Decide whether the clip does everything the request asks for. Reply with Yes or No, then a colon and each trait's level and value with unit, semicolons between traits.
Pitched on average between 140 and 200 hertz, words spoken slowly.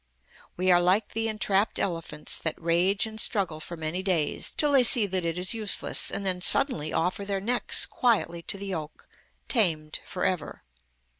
No: medium, 185 Hz; average, 175 wpm